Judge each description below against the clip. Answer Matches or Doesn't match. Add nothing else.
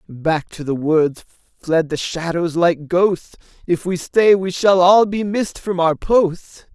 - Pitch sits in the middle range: Matches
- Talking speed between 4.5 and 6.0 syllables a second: Doesn't match